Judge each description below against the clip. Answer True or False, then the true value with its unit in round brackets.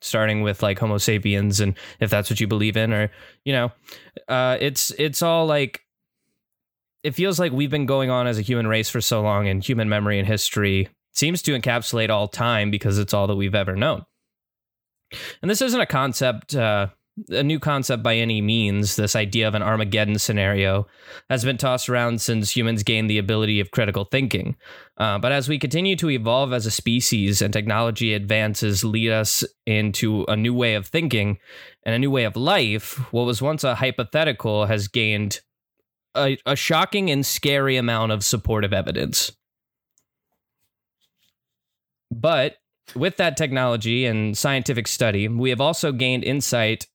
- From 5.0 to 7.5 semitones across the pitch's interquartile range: False (3.8 semitones)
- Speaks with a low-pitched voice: True (115 Hz)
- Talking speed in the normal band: True (175 wpm)